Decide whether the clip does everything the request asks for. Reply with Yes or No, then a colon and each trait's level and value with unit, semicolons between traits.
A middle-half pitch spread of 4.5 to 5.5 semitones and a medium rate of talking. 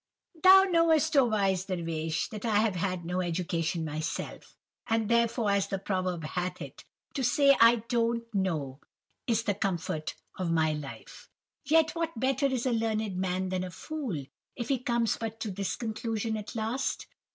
Yes: average, 4.8 semitones; average, 170 wpm